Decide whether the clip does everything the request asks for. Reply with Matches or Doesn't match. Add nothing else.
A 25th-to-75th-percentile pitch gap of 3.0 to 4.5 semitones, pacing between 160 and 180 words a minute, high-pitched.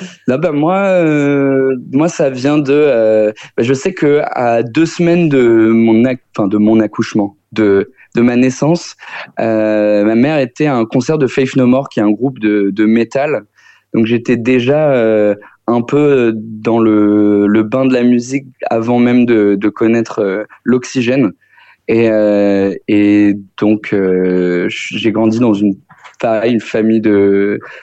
Doesn't match